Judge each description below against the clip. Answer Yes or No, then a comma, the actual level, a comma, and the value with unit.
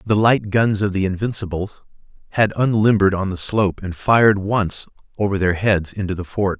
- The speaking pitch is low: Yes, low, 100 Hz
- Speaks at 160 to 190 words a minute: Yes, average, 180 wpm